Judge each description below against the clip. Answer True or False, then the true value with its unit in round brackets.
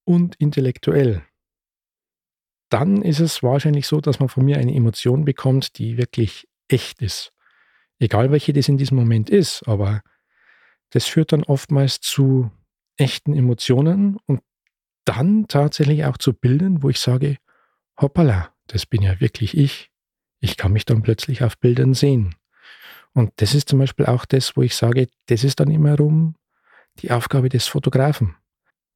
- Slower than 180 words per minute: True (155 wpm)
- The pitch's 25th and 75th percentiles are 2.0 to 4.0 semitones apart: True (3.3 semitones)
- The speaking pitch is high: False (135 Hz)